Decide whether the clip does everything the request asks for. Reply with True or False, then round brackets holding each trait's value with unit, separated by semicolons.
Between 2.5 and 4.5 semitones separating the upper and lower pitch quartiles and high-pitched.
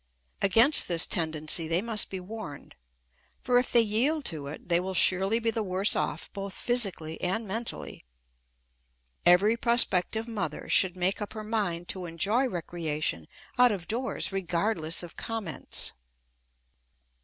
False (4.9 semitones; 195 Hz)